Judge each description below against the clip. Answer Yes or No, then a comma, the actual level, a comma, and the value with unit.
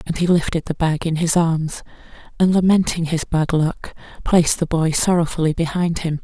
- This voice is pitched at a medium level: Yes, medium, 165 Hz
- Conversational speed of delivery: Yes, average, 185 wpm